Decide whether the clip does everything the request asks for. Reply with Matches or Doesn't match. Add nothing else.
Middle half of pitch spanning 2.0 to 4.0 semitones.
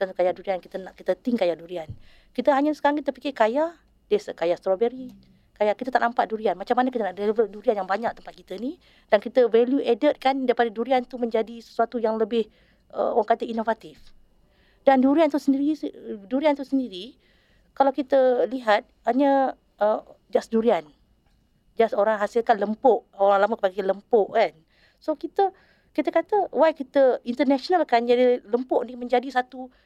Doesn't match